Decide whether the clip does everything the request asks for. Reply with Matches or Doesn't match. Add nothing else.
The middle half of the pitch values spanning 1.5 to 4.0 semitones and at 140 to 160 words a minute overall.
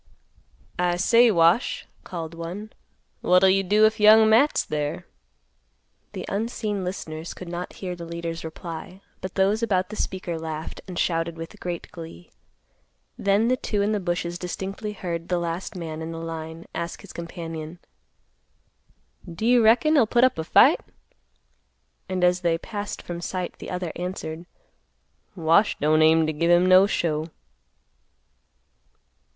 Matches